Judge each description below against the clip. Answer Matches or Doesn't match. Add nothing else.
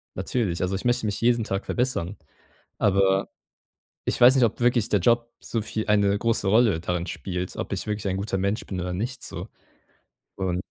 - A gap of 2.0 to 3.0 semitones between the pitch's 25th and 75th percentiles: Doesn't match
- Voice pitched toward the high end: Doesn't match